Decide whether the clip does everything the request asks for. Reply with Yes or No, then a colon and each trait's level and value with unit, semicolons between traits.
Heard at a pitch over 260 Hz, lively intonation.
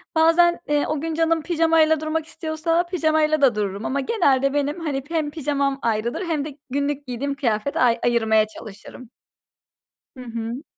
No: very high, 290 Hz; average, 4.3 semitones